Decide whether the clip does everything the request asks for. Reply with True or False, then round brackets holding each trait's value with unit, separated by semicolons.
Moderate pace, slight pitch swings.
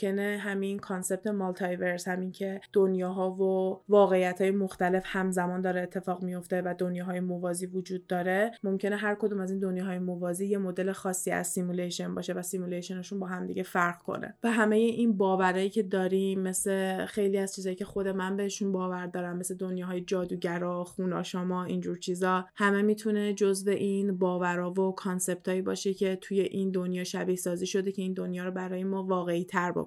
False (175 wpm; 1.3 semitones)